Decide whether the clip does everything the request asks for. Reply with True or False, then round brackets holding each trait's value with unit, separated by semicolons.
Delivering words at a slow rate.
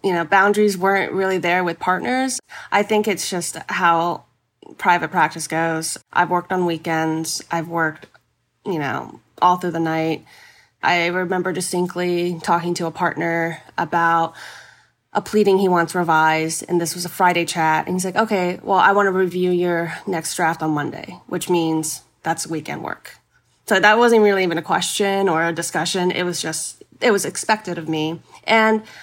False (175 wpm)